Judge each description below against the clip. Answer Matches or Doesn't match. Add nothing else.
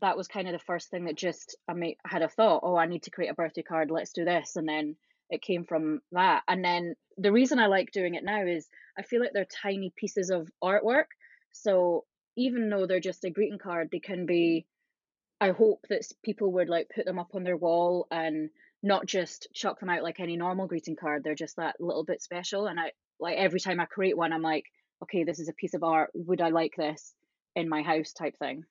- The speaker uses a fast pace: Matches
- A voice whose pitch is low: Doesn't match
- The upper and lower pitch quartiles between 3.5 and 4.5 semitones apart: Doesn't match